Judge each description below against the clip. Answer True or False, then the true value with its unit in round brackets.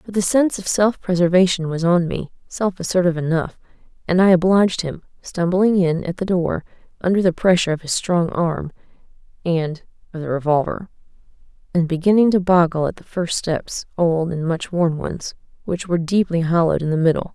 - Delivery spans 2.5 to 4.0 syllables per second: False (5.5 syllables/s)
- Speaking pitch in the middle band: True (175 Hz)